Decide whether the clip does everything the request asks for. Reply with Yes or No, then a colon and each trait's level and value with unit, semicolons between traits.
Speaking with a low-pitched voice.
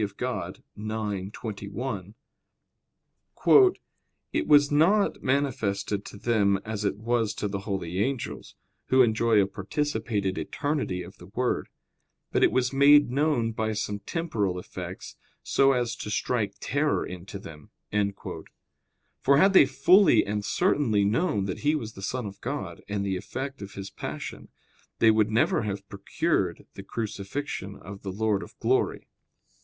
Yes: low, 110 Hz